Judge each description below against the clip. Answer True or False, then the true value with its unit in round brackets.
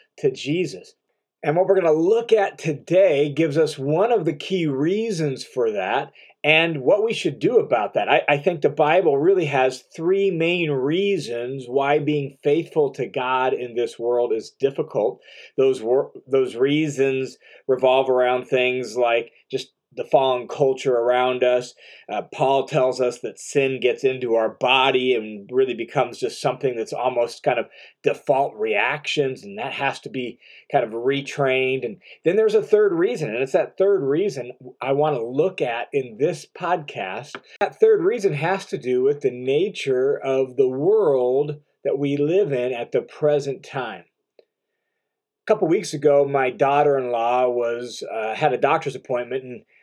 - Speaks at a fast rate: False (170 wpm)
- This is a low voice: False (145 Hz)